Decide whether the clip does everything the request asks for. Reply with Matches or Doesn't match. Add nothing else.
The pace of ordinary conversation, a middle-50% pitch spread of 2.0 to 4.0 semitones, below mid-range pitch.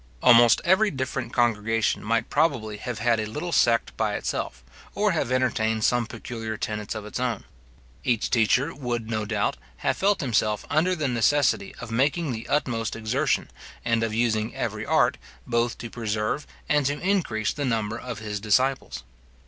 Matches